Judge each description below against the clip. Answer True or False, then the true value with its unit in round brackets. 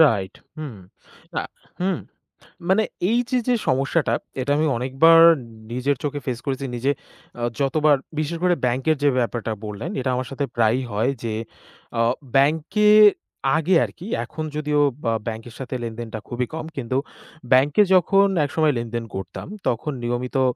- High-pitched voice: False (135 Hz)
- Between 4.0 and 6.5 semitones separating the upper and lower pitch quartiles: True (4.8 semitones)